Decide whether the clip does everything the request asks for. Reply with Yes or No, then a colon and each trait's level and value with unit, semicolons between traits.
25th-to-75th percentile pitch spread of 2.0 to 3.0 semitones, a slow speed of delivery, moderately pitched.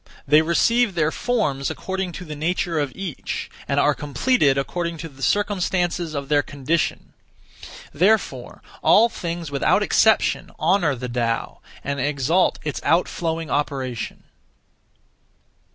No: average, 4.1 semitones; slow, 125 wpm; medium, 160 Hz